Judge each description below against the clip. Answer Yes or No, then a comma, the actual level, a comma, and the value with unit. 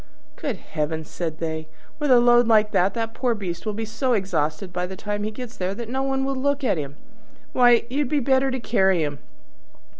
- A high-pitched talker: Yes, high, 220 Hz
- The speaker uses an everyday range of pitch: No, wide, 5.9 semitones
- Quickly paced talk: Yes, fast, 215 wpm